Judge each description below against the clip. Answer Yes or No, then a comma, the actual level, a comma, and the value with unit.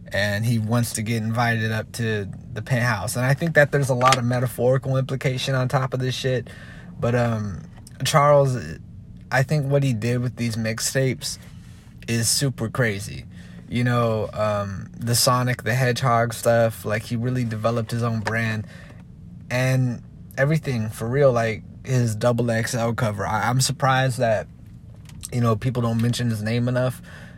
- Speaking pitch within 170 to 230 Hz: No, low, 120 Hz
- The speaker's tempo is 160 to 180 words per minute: Yes, average, 165 wpm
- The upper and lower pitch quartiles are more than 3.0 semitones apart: No, narrow, 2.4 semitones